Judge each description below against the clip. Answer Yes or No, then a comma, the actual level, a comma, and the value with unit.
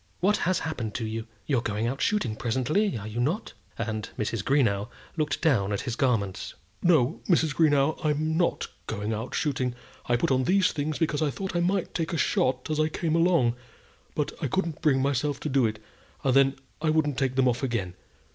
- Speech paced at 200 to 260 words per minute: Yes, fast, 205 wpm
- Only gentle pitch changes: No, average, 5.1 semitones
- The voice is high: No, low, 135 Hz